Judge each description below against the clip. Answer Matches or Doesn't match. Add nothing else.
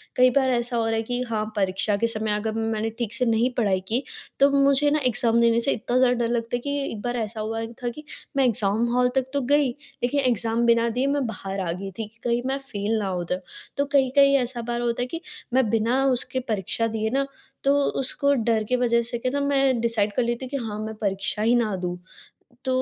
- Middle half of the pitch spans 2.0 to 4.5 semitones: Matches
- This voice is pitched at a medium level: Doesn't match